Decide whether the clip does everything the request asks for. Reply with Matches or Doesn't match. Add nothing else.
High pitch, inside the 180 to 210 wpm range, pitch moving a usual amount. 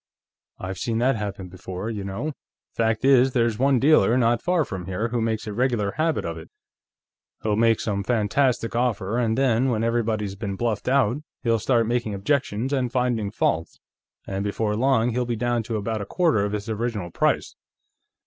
Doesn't match